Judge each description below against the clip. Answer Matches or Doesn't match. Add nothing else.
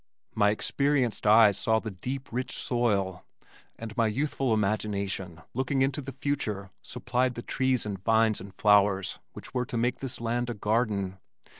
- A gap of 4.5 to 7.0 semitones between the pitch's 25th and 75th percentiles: Doesn't match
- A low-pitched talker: Matches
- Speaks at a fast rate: Doesn't match